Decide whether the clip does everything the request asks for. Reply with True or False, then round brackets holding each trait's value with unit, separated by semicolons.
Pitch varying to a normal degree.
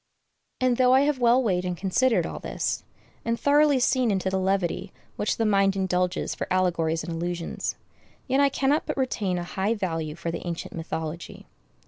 False (6.2 semitones)